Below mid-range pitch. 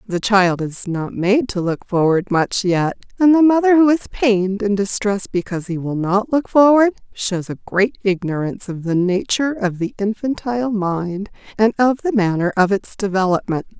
No: high, 205 Hz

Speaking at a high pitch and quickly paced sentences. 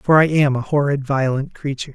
No: medium, 140 Hz; fast, 215 wpm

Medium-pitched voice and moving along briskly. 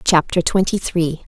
No: medium, 170 Hz; slow, 135 wpm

